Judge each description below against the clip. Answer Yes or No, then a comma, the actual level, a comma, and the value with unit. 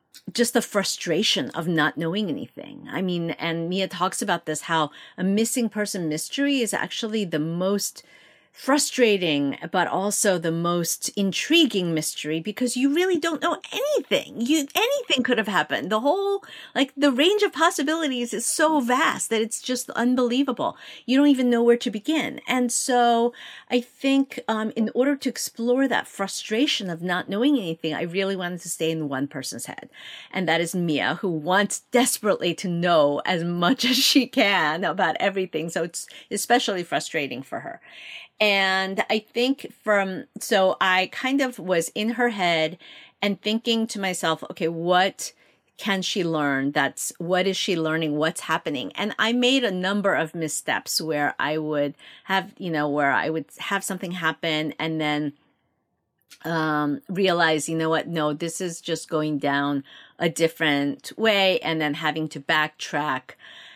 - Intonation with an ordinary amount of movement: No, wide, 7.0 semitones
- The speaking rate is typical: Yes, average, 165 wpm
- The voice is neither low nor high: No, high, 195 Hz